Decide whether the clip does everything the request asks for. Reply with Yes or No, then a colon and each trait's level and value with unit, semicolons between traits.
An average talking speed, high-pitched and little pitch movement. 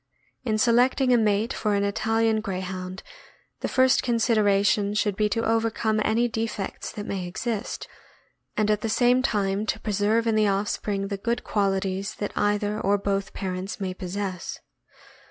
Yes: average, 155 wpm; high, 210 Hz; narrow, 2.2 semitones